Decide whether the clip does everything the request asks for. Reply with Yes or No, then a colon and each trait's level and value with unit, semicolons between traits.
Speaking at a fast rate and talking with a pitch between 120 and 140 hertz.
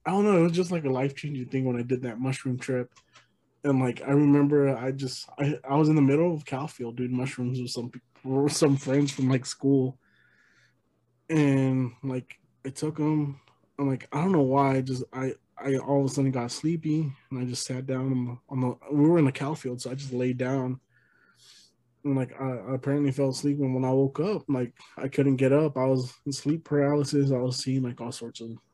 Yes: fast, 235 wpm; low, 135 Hz